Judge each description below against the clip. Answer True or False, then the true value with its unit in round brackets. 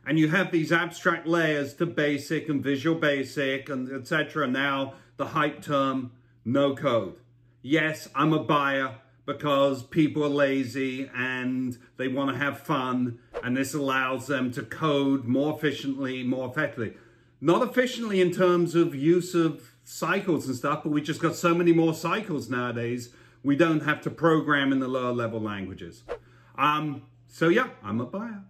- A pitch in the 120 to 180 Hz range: True (140 Hz)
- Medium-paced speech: True (165 wpm)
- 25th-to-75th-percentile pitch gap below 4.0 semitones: True (3.6 semitones)